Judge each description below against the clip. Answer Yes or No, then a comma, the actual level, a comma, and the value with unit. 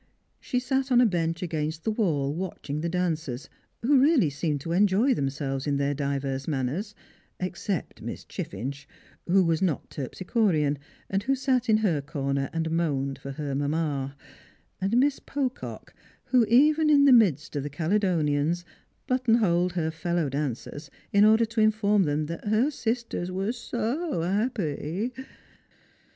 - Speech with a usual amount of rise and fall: No, wide, 7.2 semitones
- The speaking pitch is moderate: Yes, medium, 175 Hz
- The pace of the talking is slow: No, average, 150 wpm